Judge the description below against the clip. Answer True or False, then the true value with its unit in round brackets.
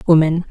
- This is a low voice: False (165 Hz)